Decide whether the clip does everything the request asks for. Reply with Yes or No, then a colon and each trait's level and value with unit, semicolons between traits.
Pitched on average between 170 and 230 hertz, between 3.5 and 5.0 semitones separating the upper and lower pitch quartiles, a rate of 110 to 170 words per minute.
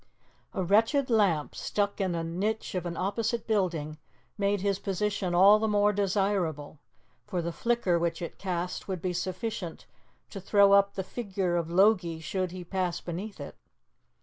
No: high, 190 Hz; average, 2.9 semitones; average, 165 wpm